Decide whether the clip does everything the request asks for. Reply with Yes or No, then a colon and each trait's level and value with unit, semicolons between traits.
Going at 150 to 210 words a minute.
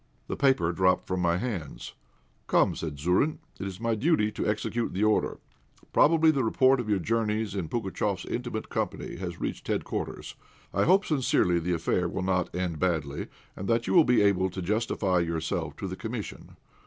Yes: average, 180 wpm